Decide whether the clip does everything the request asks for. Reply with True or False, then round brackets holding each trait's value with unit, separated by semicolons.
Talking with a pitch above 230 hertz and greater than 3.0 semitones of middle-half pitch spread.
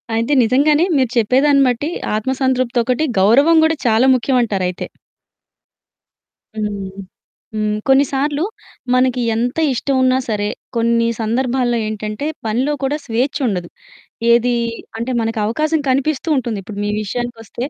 True (245 Hz; 3.5 semitones)